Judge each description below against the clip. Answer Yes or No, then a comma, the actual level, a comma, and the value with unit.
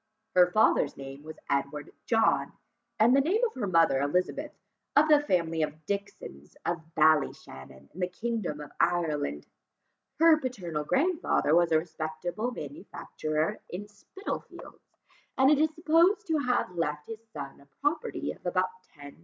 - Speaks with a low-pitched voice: No, medium, 180 Hz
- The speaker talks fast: No, average, 150 wpm